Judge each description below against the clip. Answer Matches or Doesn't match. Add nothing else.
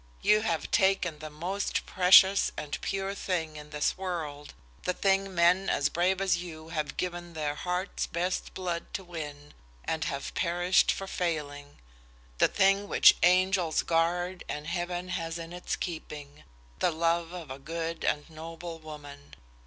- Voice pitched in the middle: Matches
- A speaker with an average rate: Matches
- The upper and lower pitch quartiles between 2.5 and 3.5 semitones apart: Matches